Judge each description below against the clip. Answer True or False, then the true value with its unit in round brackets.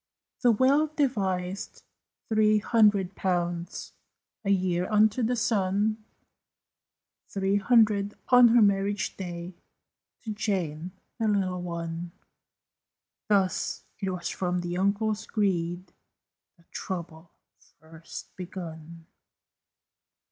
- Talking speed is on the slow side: True (95 wpm)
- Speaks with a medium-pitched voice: False (195 Hz)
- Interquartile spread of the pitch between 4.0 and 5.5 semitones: False (3.4 semitones)